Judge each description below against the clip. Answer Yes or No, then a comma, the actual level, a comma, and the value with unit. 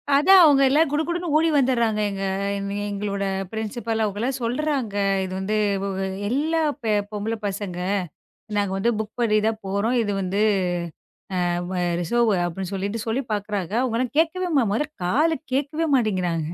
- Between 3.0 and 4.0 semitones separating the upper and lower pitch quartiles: No, wide, 5.5 semitones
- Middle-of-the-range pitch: No, high, 225 Hz